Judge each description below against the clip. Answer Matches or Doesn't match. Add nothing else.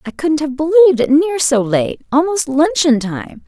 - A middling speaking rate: Matches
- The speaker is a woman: Matches